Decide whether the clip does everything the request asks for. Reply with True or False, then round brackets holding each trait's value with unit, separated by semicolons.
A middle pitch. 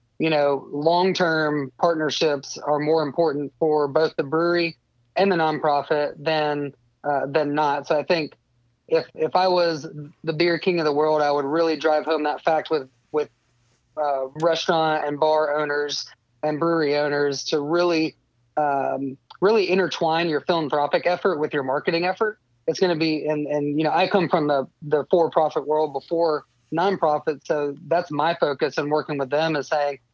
True (155 Hz)